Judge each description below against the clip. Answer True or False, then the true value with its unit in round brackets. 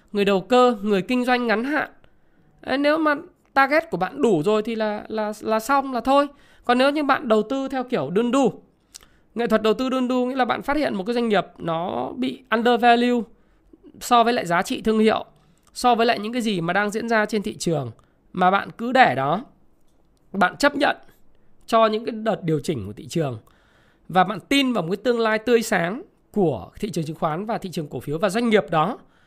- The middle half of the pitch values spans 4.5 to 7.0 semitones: True (5.1 semitones)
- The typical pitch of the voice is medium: False (220 Hz)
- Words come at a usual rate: True (230 wpm)